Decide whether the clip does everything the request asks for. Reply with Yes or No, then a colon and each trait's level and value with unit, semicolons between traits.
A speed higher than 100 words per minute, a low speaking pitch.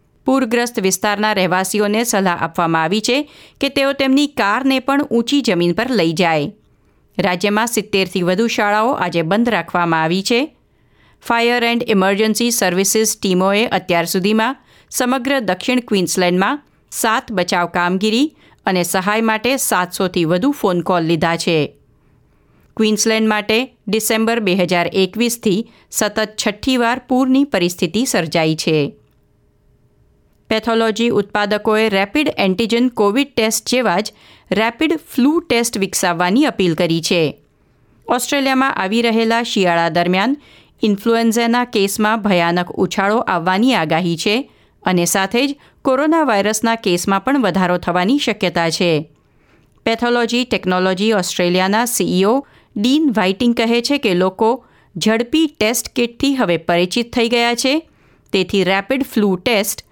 No: average, 120 wpm; high, 215 Hz